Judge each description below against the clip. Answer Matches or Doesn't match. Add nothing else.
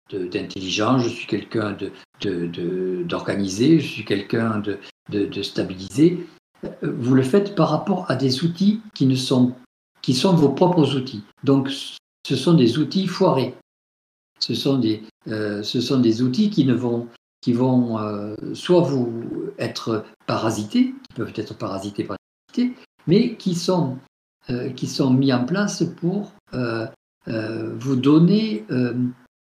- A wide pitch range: Matches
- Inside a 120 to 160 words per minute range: Matches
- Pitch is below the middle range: Matches